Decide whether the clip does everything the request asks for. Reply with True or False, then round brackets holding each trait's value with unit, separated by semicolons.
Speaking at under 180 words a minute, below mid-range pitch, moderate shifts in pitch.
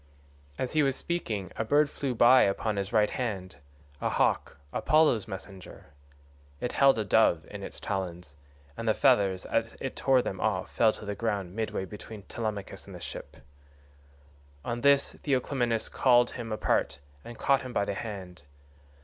True (165 wpm; 110 Hz; 4.2 semitones)